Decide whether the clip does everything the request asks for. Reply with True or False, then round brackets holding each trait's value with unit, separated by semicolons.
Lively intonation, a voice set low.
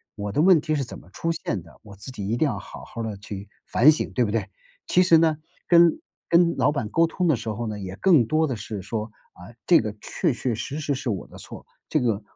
True (7.1 semitones; 120 Hz)